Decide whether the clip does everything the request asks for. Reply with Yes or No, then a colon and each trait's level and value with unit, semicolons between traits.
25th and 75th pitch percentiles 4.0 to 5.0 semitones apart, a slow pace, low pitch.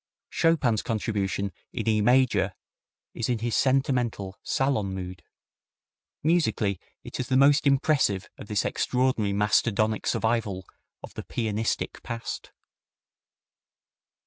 Yes: average, 4.3 semitones; slow, 110 wpm; low, 115 Hz